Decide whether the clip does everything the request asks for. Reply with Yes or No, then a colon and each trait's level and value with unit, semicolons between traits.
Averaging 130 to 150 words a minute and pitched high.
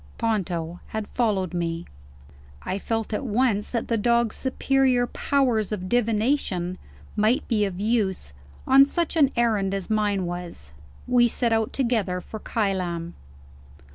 Yes: average, 140 wpm; high, 215 Hz